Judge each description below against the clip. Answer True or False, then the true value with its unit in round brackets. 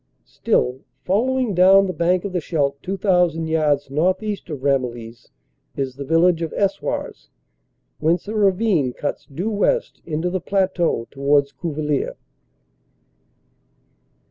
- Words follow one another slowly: True (120 wpm)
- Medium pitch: True (165 Hz)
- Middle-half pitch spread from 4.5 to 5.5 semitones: True (5.1 semitones)